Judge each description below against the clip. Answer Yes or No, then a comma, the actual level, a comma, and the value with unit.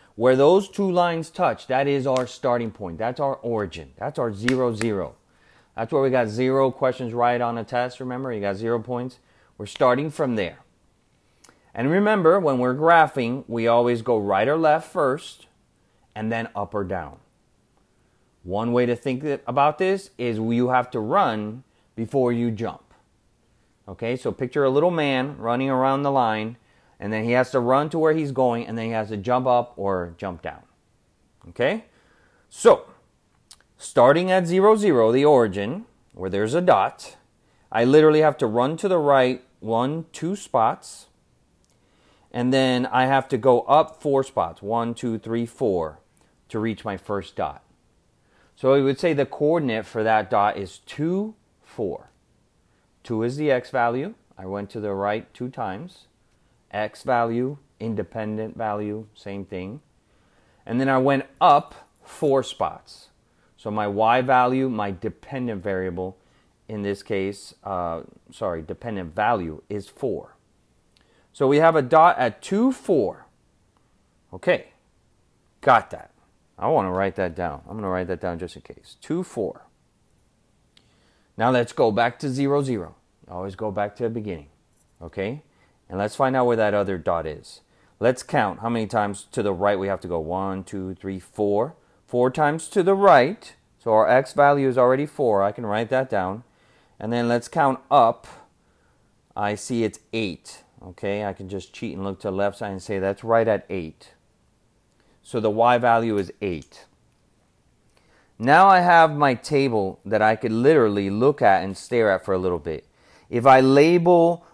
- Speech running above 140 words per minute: Yes, average, 170 wpm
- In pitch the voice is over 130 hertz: No, low, 115 Hz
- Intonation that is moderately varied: Yes, average, 4.6 semitones